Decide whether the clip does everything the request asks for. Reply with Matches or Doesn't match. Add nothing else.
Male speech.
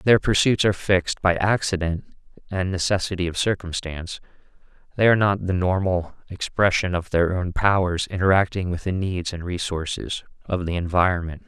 Matches